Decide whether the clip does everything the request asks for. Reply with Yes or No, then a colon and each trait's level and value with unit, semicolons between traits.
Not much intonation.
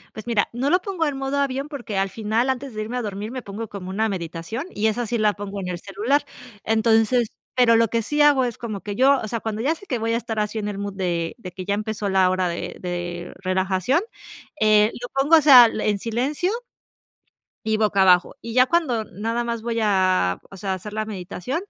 No: average, 3.8 semitones